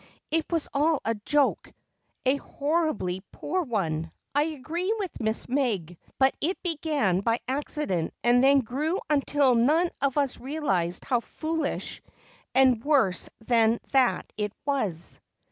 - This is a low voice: No, very high, 270 Hz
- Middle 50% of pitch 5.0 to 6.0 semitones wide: Yes, wide, 5.4 semitones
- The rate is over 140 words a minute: No, slow, 135 wpm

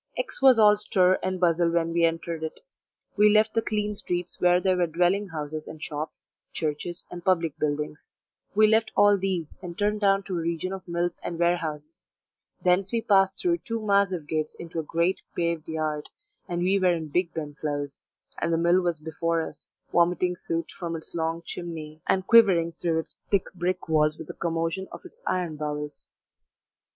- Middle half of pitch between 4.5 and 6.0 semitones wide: No, average, 2.9 semitones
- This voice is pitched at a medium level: Yes, medium, 170 Hz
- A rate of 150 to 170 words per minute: No, average, 185 wpm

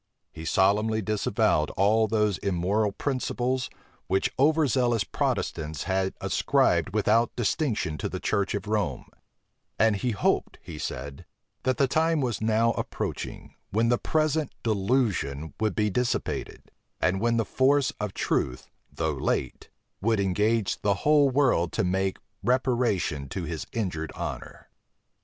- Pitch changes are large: No, average, 4.6 semitones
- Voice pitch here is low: Yes, low, 110 Hz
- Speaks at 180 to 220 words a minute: No, average, 140 wpm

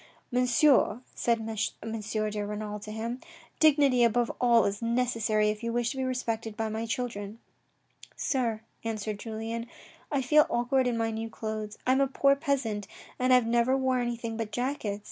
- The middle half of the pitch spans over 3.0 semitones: No, narrow, 2.5 semitones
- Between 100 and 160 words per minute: No, average, 185 wpm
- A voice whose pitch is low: No, high, 230 Hz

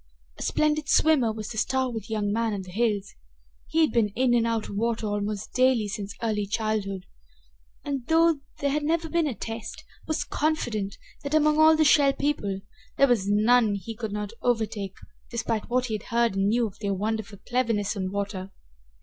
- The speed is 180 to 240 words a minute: Yes, average, 190 wpm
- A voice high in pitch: Yes, high, 225 Hz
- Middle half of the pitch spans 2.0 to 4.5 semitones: Yes, average, 4.2 semitones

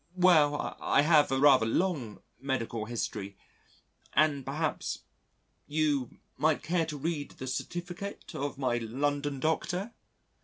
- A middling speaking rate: No, slow, 120 wpm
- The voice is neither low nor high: Yes, medium, 145 Hz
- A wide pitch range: No, average, 3.4 semitones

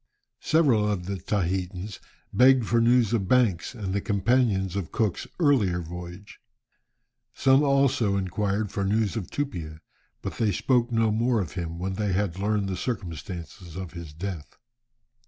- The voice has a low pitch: Yes, low, 100 Hz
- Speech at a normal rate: Yes, average, 155 wpm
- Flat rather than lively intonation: No, average, 4.3 semitones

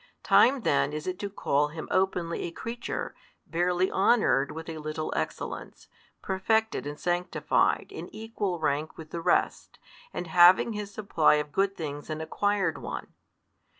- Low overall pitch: No, medium, 175 Hz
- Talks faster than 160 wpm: No, average, 150 wpm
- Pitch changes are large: No, average, 4.3 semitones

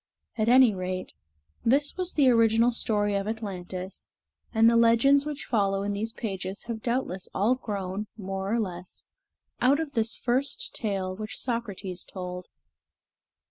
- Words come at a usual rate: Yes, average, 145 wpm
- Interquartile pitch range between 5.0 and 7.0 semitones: No, average, 3.7 semitones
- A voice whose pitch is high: Yes, high, 220 Hz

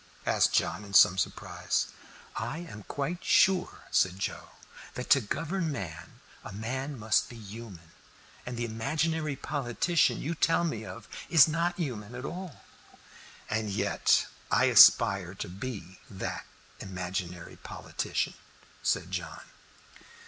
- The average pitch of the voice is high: No, low, 120 Hz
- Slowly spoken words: Yes, slow, 130 wpm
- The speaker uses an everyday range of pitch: No, wide, 7.8 semitones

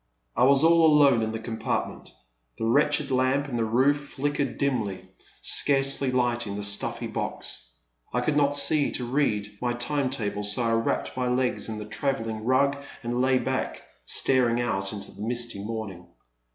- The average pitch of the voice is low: Yes, low, 125 Hz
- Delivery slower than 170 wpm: No, average, 175 wpm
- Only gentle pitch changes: No, average, 3.9 semitones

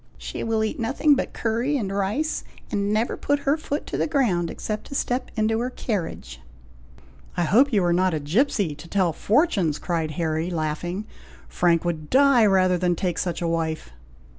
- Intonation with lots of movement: Yes, wide, 6.3 semitones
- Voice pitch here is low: No, high, 195 Hz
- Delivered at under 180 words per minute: No, average, 185 wpm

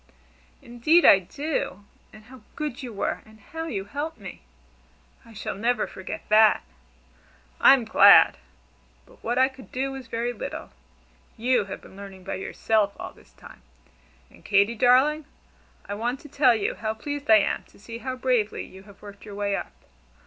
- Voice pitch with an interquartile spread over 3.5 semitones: Yes, average, 4.2 semitones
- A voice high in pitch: Yes, high, 230 Hz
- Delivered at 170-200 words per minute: Yes, average, 175 wpm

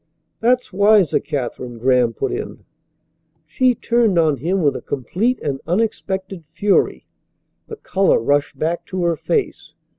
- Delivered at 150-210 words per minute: No, average, 140 wpm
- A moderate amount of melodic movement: No, wide, 6.7 semitones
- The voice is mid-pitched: Yes, medium, 175 Hz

